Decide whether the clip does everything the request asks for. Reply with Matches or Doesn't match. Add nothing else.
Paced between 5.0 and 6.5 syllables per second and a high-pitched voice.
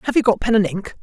Doesn't match